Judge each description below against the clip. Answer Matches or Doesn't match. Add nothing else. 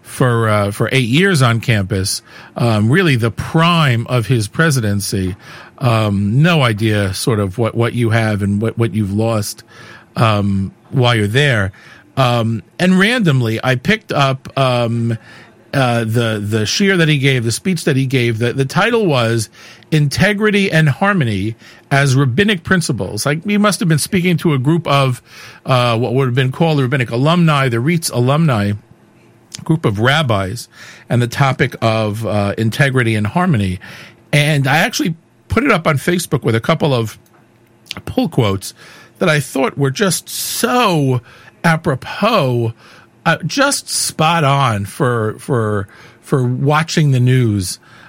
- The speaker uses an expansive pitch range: Matches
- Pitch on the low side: Matches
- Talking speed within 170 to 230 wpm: Doesn't match